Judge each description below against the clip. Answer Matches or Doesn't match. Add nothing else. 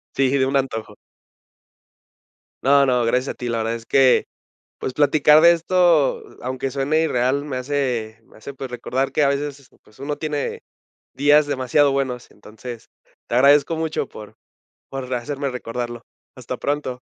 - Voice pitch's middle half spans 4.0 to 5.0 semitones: Doesn't match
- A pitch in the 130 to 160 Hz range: Matches